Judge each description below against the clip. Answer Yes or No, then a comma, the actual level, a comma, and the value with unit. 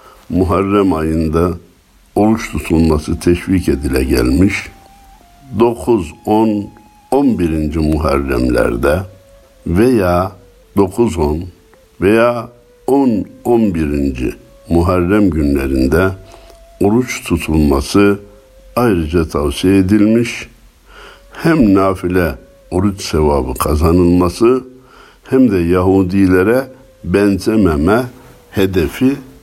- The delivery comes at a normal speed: No, slow, 70 wpm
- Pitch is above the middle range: No, very low, 95 Hz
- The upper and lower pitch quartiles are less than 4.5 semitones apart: No, average, 5.3 semitones